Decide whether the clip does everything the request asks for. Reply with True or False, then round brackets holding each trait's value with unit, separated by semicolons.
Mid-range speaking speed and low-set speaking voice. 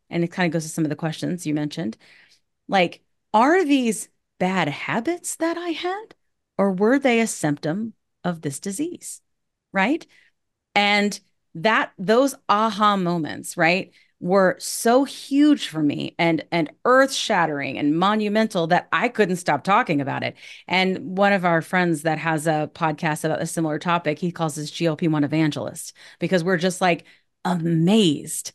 False (160 wpm; 180 Hz)